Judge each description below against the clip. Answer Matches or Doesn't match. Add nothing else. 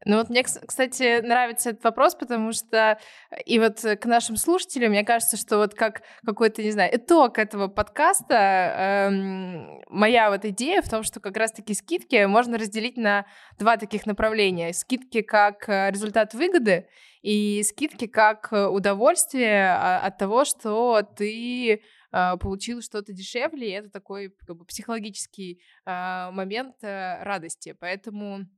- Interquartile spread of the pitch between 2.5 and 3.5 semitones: Matches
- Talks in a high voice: Matches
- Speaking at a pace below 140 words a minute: Matches